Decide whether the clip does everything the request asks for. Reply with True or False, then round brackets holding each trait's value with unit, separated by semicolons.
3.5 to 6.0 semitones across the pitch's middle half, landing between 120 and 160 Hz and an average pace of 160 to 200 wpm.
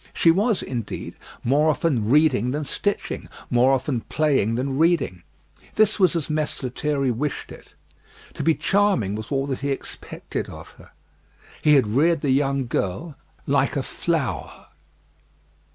False (4.0 semitones; 140 Hz; 150 wpm)